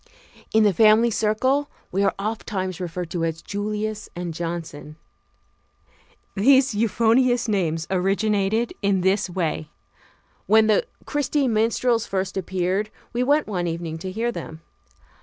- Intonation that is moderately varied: Yes, average, 4.1 semitones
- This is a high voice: Yes, high, 205 Hz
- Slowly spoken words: Yes, slow, 130 wpm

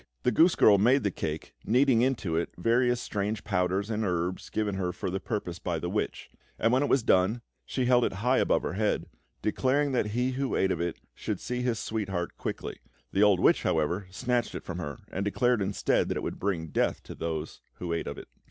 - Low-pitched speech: Yes, low, 105 Hz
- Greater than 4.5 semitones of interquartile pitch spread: Yes, average, 5.3 semitones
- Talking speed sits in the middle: No, fast, 220 wpm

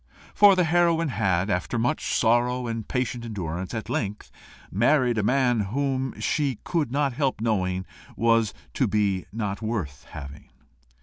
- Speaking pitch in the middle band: No, low, 115 Hz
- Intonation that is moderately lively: Yes, average, 4.7 semitones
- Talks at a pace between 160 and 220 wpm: No, average, 140 wpm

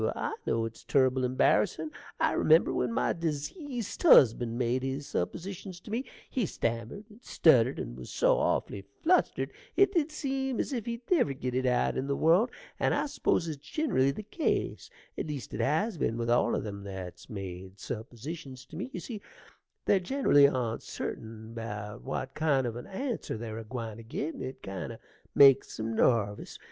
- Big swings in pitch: Yes, wide, 8.9 semitones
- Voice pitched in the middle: No, low, 130 Hz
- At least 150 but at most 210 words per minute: Yes, average, 180 wpm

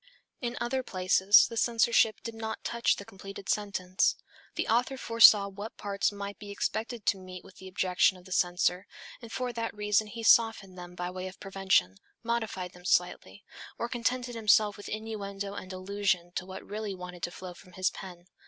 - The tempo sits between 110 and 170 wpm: No, average, 185 wpm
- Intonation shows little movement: No, average, 3.3 semitones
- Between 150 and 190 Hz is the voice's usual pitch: No, high, 200 Hz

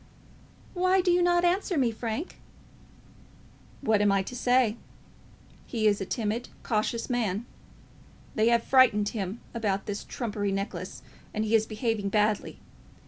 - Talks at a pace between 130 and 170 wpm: Yes, average, 140 wpm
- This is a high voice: Yes, high, 225 Hz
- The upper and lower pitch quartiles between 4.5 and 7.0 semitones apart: No, average, 3.2 semitones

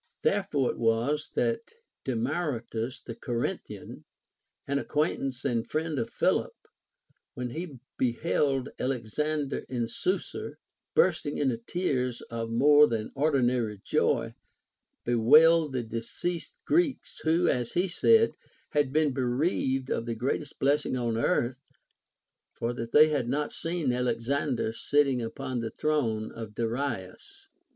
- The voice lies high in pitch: No, low, 130 Hz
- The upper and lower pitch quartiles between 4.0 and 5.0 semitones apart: Yes, average, 4.4 semitones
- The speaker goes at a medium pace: No, slow, 130 wpm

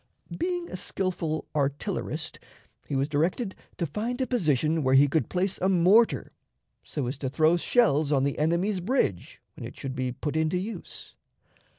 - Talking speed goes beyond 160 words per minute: Yes, average, 170 wpm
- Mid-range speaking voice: Yes, medium, 160 Hz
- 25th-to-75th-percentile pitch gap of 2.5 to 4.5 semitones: No, average, 5.1 semitones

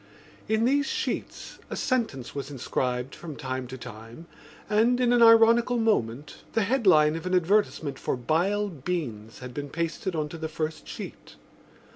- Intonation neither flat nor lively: No, wide, 8.8 semitones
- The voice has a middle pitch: Yes, medium, 160 Hz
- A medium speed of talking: Yes, average, 160 wpm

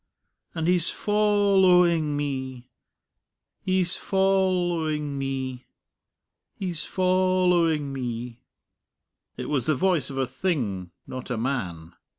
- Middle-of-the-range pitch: Yes, medium, 155 Hz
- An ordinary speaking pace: No, slow, 115 wpm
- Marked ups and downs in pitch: Yes, wide, 5.9 semitones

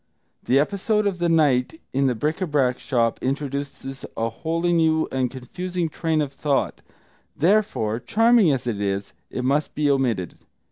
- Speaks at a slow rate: No, average, 160 wpm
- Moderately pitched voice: Yes, medium, 145 Hz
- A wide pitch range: No, average, 4.7 semitones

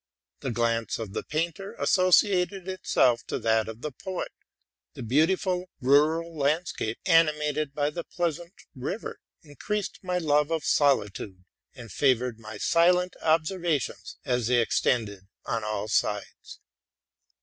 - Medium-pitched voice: Yes, medium, 150 Hz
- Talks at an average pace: No, slow, 130 wpm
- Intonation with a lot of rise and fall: Yes, wide, 6.7 semitones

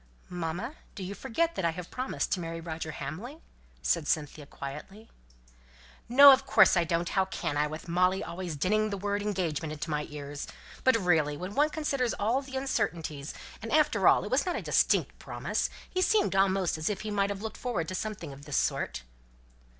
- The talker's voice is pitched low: No, high, 190 Hz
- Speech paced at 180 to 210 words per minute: Yes, average, 195 wpm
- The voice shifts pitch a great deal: Yes, wide, 5.9 semitones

